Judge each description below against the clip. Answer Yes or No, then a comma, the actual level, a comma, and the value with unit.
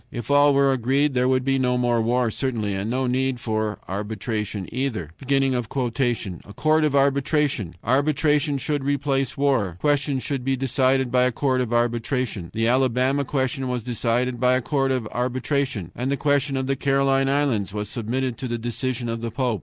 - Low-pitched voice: Yes, low, 130 Hz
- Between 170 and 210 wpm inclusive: Yes, average, 180 wpm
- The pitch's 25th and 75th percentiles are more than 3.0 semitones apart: No, average, 2.7 semitones